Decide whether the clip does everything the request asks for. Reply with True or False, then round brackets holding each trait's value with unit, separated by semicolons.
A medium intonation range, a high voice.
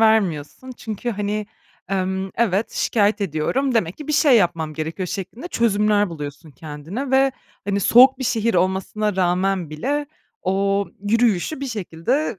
True (4.6 semitones; 205 Hz)